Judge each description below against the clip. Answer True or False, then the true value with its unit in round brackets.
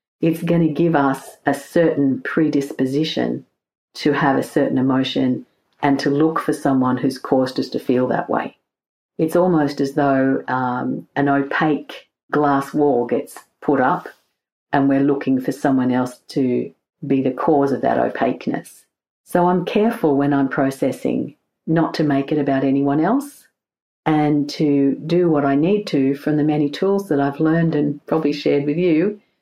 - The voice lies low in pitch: False (145 Hz)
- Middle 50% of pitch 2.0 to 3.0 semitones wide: True (2.6 semitones)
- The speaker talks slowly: False (165 wpm)